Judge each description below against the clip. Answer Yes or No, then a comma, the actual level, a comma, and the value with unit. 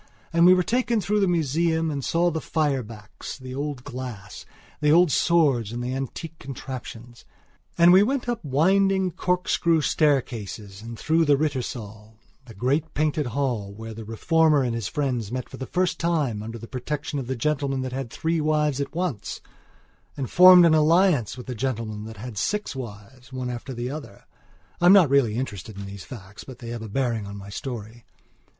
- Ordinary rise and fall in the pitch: No, wide, 5.7 semitones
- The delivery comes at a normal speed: Yes, average, 190 wpm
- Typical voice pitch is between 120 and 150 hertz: Yes, low, 135 Hz